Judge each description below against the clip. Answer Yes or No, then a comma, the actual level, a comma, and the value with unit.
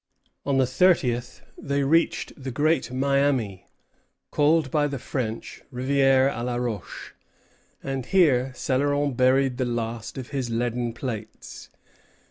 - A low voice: Yes, low, 130 Hz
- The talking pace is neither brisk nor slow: No, slow, 125 wpm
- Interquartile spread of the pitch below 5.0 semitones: Yes, narrow, 2.5 semitones